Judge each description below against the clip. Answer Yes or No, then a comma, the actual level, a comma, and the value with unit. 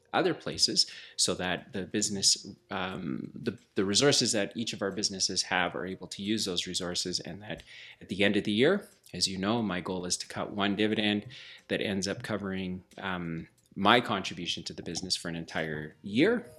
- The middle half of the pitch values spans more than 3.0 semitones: No, average, 2.7 semitones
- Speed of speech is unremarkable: Yes, average, 195 wpm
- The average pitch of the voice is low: Yes, very low, 95 Hz